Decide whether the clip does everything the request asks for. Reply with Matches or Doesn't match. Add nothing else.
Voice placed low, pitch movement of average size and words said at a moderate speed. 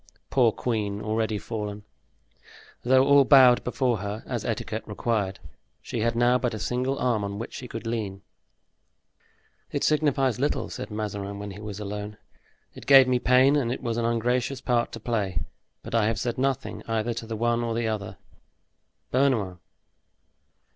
Matches